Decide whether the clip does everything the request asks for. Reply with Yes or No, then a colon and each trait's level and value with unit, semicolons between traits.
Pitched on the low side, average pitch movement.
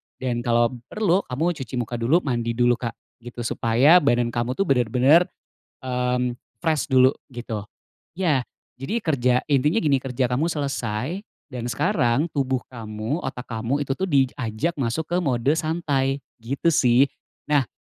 Yes: low, 130 Hz; average, 3.8 semitones